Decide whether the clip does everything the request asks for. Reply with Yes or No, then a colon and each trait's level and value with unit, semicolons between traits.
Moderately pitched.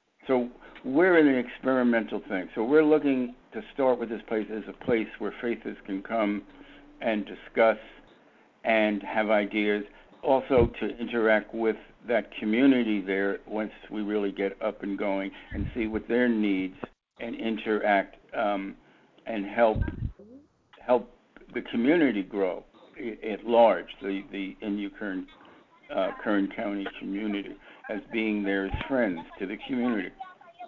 No: low, 110 Hz